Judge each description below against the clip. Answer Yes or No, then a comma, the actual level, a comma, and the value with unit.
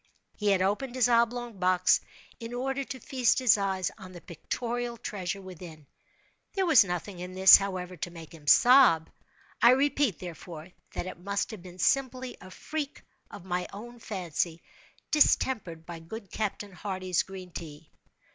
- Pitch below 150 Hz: No, high, 195 Hz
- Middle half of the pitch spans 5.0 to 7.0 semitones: Yes, average, 5.3 semitones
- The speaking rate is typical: Yes, average, 160 wpm